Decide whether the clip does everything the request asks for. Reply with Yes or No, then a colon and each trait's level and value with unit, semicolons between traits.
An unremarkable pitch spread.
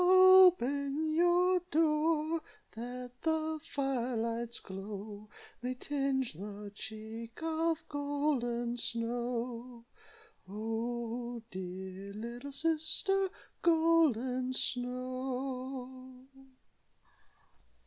Yes: average, 4.9 semitones